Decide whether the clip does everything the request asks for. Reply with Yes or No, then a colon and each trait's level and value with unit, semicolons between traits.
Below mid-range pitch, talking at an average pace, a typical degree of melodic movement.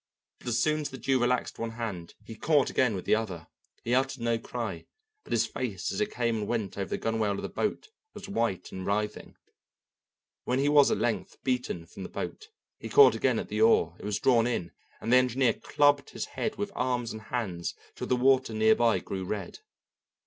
No: low, 120 Hz; fast, 215 wpm; average, 3.7 semitones